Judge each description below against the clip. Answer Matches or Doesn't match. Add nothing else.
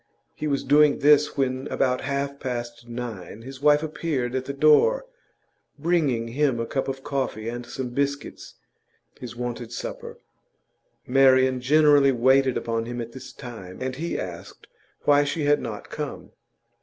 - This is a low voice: Matches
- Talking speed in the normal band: Matches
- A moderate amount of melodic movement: Matches